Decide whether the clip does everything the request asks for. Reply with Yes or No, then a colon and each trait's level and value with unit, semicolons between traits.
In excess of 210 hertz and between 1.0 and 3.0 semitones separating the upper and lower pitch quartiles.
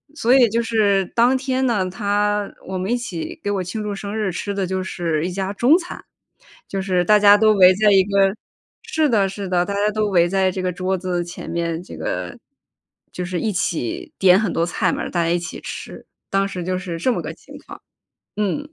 No: high, 195 Hz; narrow, 2.5 semitones